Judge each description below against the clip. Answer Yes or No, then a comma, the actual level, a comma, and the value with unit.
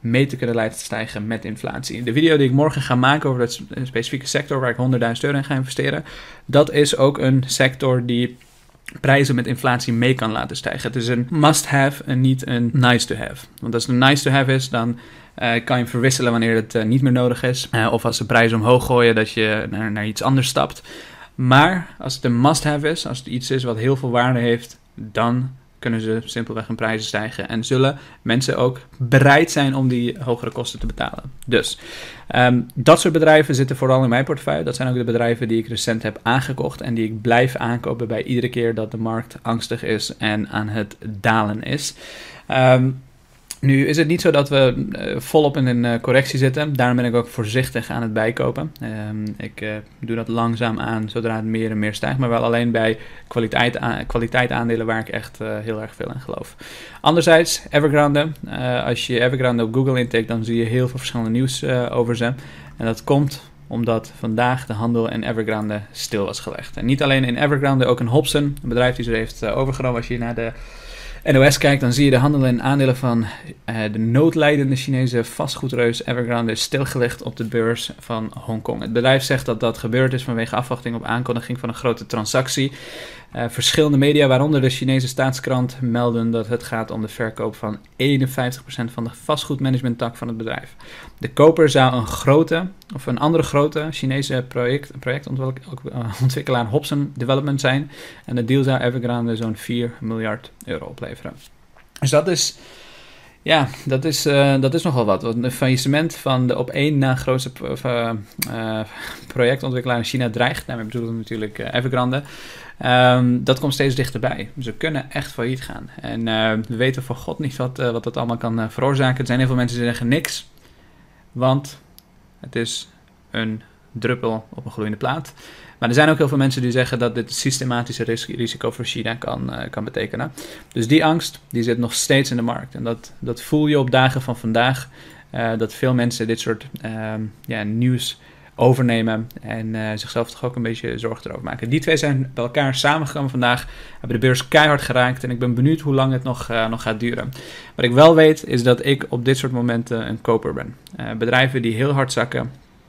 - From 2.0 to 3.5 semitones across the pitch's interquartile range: Yes, narrow, 2.6 semitones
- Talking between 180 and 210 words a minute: Yes, fast, 200 wpm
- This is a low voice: Yes, low, 125 Hz